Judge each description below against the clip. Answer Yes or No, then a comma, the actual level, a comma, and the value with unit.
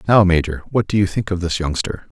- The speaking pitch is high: No, very low, 95 Hz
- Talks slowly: No, fast, 245 wpm